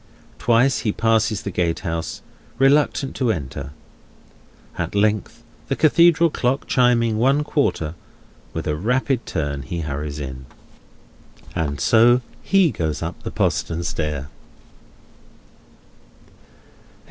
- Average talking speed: No, slow, 110 wpm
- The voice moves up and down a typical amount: No, wide, 8.4 semitones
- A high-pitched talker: No, low, 105 Hz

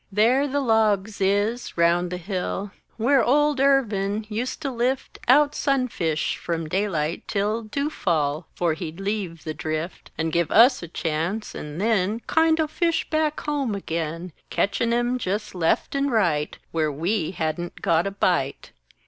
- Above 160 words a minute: No, average, 155 wpm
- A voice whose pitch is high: Yes, high, 200 Hz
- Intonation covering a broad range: Yes, wide, 6.7 semitones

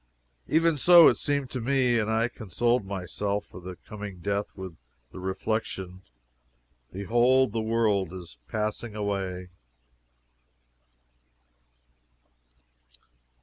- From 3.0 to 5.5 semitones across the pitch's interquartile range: Yes, average, 4.1 semitones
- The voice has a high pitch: No, low, 105 Hz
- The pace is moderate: No, slow, 105 wpm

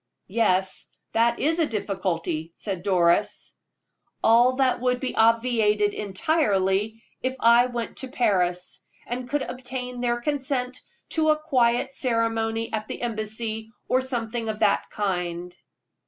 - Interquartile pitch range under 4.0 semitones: Yes, average, 3.5 semitones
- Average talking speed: No, slow, 130 wpm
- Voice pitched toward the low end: No, high, 230 Hz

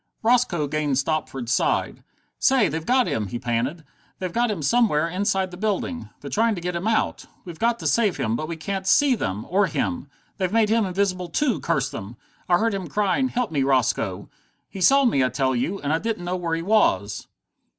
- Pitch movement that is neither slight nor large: No, wide, 7.2 semitones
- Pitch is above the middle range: No, medium, 180 Hz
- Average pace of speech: No, fast, 210 wpm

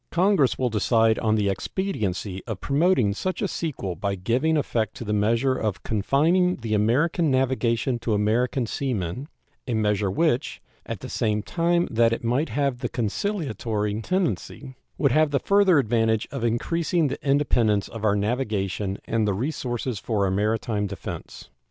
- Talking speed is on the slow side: No, average, 165 wpm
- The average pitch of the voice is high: No, low, 115 Hz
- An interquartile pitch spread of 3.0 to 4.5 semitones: No, average, 5.3 semitones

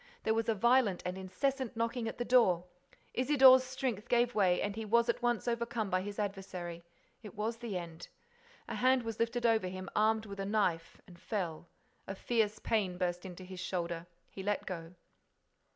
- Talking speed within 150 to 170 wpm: No, average, 190 wpm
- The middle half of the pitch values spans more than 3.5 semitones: Yes, average, 4.2 semitones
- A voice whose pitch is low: No, high, 210 Hz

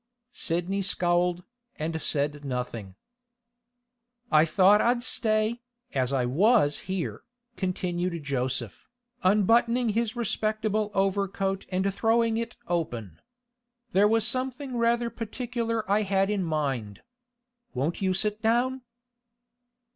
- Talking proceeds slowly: Yes, slow, 110 wpm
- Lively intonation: Yes, wide, 5.9 semitones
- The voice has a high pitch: Yes, high, 195 Hz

